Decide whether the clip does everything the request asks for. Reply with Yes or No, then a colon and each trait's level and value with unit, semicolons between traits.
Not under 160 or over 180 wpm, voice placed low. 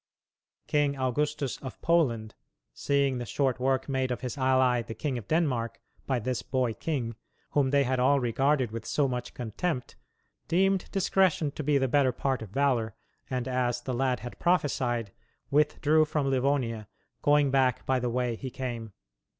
Yes: average, 165 wpm; low, 130 Hz